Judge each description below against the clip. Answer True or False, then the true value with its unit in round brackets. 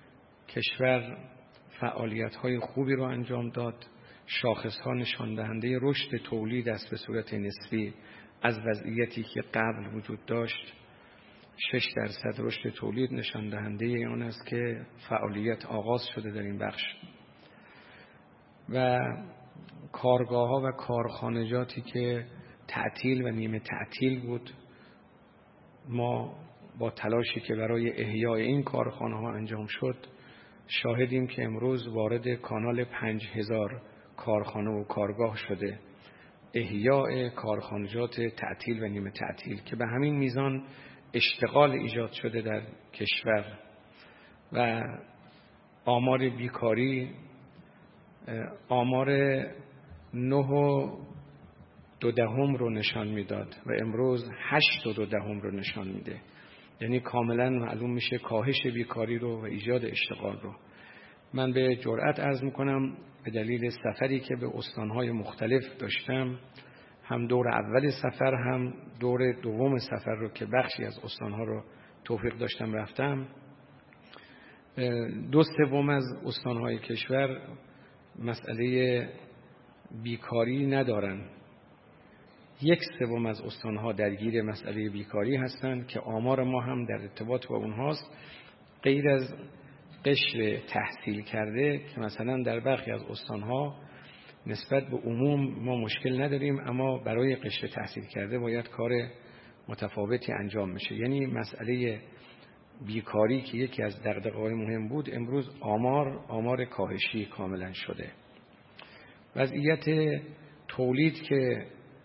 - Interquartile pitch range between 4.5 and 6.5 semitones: False (2.8 semitones)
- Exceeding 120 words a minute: False (115 wpm)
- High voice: False (120 Hz)